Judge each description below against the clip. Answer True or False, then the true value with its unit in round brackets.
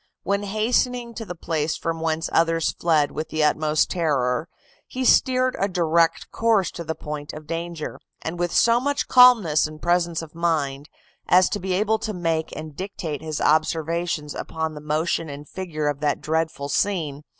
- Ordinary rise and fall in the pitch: True (3.4 semitones)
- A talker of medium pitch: True (165 Hz)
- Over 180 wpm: False (175 wpm)